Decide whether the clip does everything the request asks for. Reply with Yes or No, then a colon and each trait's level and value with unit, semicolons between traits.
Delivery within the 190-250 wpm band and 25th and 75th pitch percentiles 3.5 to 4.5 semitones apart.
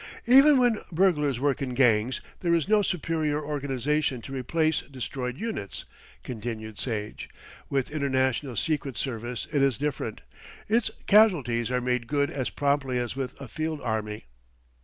No: average, 145 wpm; average, 4.1 semitones